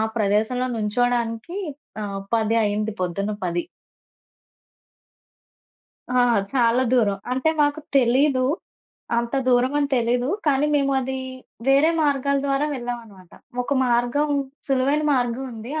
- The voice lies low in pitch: No, high, 245 Hz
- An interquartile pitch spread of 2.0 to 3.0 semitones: No, average, 3.4 semitones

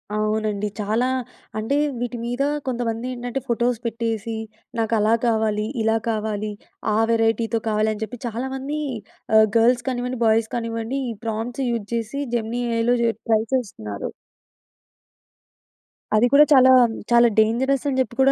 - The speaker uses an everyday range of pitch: No, narrow, 2.0 semitones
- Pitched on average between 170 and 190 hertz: No, high, 230 Hz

